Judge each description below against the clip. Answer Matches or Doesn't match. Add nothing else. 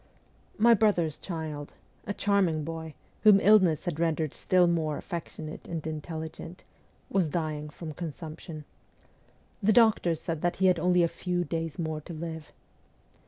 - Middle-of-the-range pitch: Matches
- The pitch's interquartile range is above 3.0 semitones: Doesn't match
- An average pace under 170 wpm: Matches